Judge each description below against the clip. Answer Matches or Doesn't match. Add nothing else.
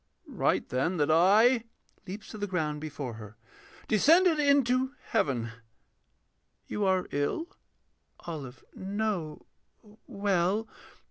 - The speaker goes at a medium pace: Doesn't match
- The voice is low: Doesn't match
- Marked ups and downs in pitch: Matches